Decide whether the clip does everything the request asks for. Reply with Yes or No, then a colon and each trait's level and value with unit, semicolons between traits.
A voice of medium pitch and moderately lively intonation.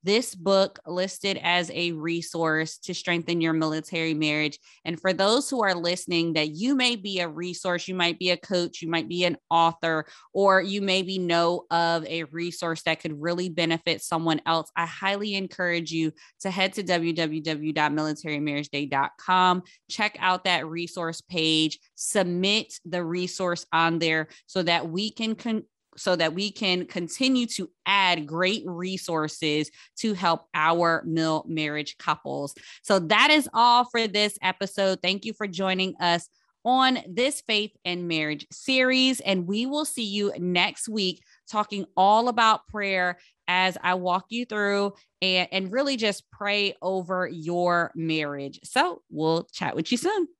Yes: medium, 180 Hz; average, 3.4 semitones